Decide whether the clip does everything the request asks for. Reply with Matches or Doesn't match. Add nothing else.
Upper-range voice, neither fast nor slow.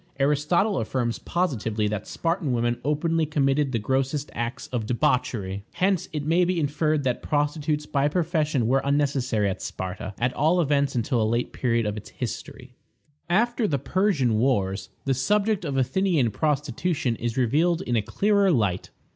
Doesn't match